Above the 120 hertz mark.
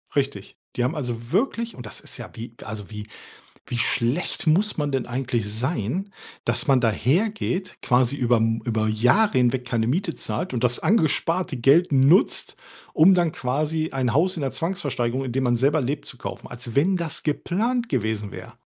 Yes: low, 135 Hz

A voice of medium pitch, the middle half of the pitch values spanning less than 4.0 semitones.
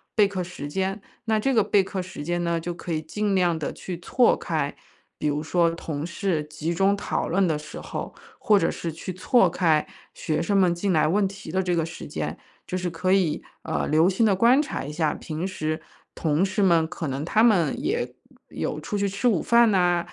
Yes: medium, 180 Hz; average, 3.5 semitones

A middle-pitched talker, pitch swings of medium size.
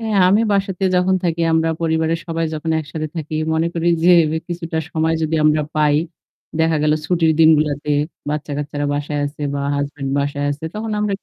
No: medium, 160 Hz; narrow, 2.2 semitones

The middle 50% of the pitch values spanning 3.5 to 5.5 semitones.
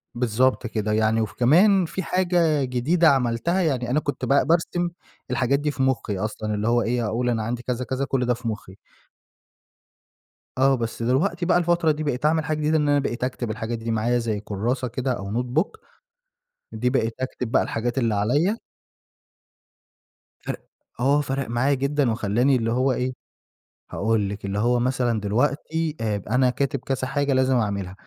Yes: average, 3.9 semitones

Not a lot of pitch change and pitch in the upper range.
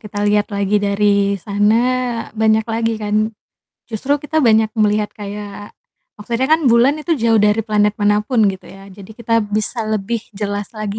Yes: narrow, 1.8 semitones; high, 210 Hz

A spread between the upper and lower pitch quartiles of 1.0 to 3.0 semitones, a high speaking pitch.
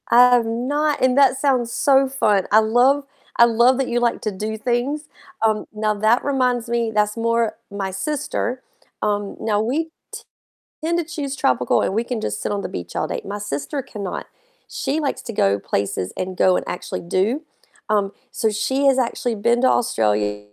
No: average, 4.3 semitones; high, 230 Hz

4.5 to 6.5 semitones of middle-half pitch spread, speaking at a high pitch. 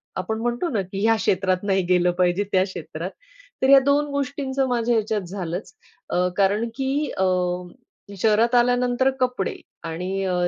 Yes: average, 5.1 semitones; high, 215 Hz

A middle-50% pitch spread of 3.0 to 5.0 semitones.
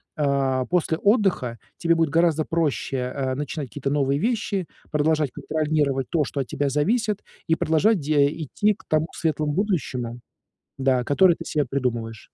Yes: average, 3.7 semitones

